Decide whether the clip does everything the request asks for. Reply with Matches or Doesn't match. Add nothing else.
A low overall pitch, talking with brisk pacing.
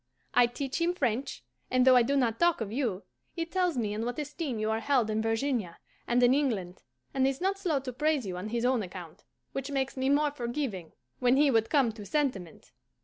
Doesn't match